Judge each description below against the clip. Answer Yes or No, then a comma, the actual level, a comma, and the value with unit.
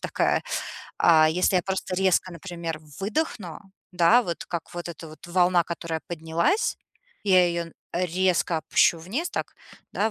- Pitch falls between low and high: Yes, medium, 175 Hz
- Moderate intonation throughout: No, narrow, 2.0 semitones